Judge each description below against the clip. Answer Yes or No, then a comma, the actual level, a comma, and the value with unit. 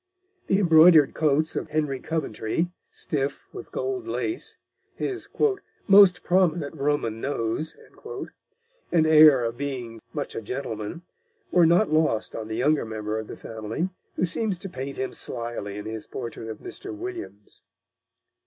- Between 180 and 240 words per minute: No, average, 145 wpm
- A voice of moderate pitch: Yes, medium, 145 Hz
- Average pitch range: No, wide, 7.2 semitones